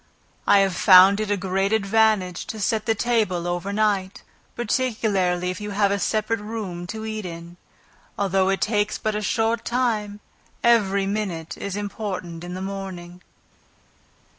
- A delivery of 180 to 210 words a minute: No, average, 155 wpm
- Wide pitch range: No, average, 2.7 semitones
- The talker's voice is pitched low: No, high, 200 Hz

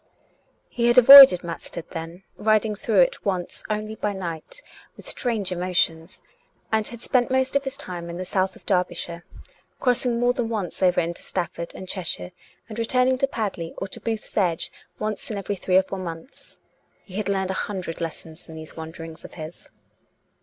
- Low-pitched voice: No, high, 190 Hz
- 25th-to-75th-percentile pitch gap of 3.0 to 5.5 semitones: Yes, average, 4.8 semitones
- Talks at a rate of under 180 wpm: No, average, 190 wpm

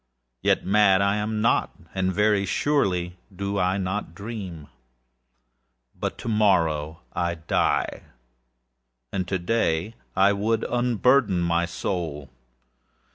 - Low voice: Yes, very low, 95 Hz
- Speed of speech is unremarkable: No, slow, 110 wpm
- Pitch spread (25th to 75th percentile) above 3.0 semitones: Yes, average, 3.6 semitones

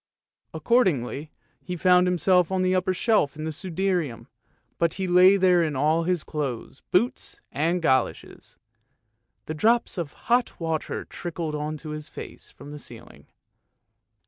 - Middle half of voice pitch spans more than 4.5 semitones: No, average, 3.4 semitones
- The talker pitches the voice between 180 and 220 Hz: No, medium, 170 Hz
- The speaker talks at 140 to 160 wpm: Yes, average, 155 wpm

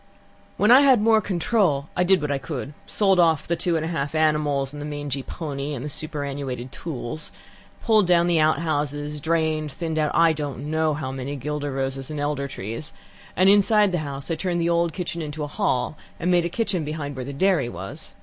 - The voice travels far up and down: No, average, 3.3 semitones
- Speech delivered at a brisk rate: Yes, fast, 210 wpm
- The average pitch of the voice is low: No, medium, 155 Hz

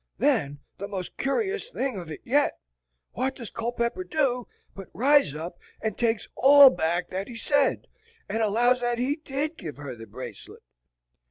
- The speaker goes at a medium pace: Yes, average, 165 wpm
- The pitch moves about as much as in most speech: No, wide, 7.4 semitones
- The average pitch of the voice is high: Yes, high, 235 Hz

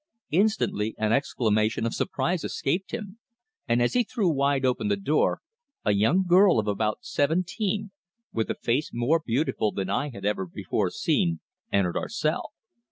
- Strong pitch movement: Yes, wide, 8.9 semitones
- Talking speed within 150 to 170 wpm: Yes, average, 165 wpm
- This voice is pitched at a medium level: No, low, 130 Hz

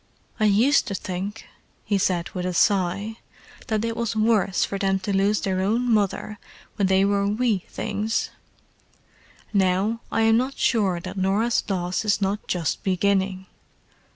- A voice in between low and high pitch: No, high, 200 Hz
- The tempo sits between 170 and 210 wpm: No, average, 155 wpm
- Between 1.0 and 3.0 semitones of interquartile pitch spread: Yes, narrow, 2.5 semitones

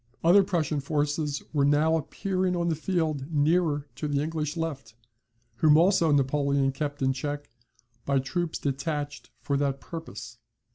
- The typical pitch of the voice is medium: Yes, medium, 150 Hz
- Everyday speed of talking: Yes, average, 145 wpm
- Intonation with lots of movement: No, narrow, 2.6 semitones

